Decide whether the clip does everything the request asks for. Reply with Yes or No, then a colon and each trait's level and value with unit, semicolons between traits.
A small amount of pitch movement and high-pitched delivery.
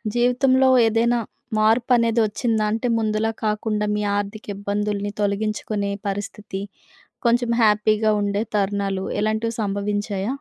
Yes: narrow, 2.0 semitones; high, 215 Hz